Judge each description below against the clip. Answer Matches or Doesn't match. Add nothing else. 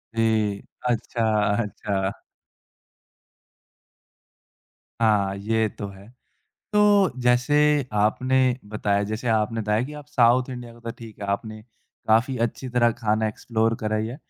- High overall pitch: Doesn't match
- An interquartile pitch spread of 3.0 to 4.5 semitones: Doesn't match